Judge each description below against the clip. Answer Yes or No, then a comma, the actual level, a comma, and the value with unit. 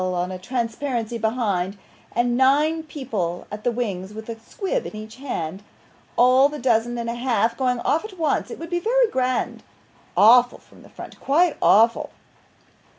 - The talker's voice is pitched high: Yes, high, 240 Hz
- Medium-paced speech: Yes, average, 170 wpm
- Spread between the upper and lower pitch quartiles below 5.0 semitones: Yes, average, 4.4 semitones